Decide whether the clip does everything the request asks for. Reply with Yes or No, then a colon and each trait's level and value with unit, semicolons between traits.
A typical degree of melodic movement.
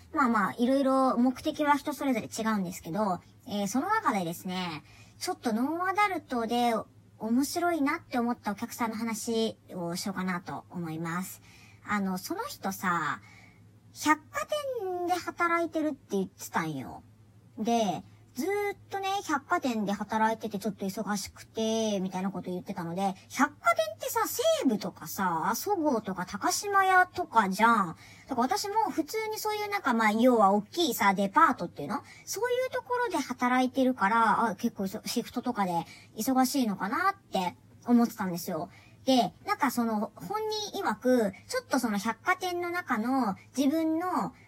No: wide, 8.3 semitones